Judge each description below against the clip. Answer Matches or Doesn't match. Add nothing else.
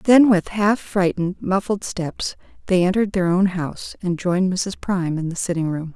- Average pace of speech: Matches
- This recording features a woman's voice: Matches